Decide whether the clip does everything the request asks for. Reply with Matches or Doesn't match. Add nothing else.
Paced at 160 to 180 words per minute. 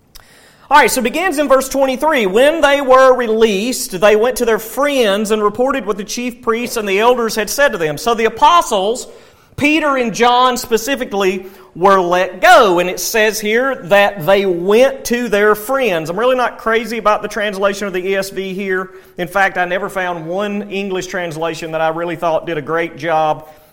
Doesn't match